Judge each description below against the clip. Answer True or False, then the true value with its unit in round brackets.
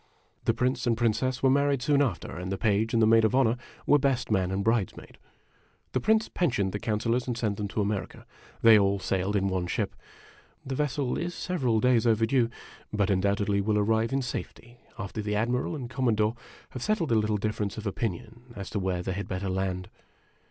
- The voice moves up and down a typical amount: True (3.8 semitones)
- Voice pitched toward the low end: True (110 Hz)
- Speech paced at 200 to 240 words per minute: True (205 wpm)